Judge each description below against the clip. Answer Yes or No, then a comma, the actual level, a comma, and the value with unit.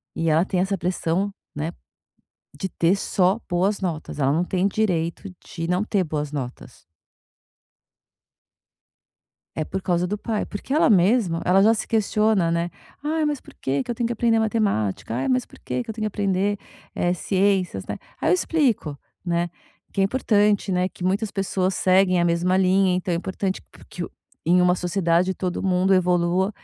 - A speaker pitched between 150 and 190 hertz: Yes, medium, 185 Hz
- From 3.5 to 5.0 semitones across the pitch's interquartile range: No, average, 3.0 semitones